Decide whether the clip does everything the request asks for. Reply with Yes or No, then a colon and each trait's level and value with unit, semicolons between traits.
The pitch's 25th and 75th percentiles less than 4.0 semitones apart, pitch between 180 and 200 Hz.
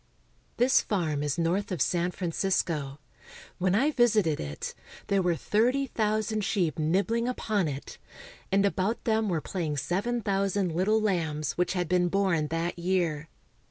No: average, 4.3 semitones; medium, 185 Hz